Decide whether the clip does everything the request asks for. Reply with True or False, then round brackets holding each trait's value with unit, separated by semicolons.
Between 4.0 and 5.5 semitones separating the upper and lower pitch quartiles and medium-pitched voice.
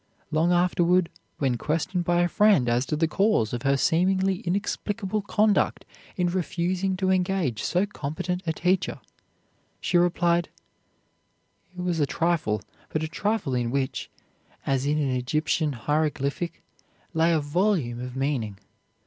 True (4.7 semitones; 170 Hz)